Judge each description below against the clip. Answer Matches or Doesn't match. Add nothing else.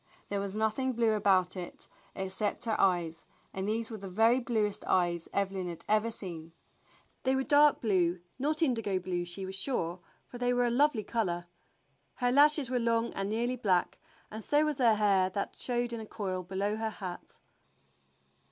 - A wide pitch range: Doesn't match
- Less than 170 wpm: Doesn't match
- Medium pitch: Doesn't match